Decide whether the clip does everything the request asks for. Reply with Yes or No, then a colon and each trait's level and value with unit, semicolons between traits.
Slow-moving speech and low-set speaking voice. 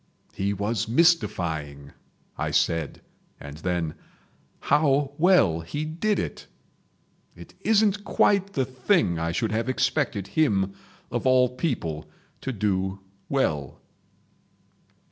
Yes: slow, 110 wpm; low, 115 Hz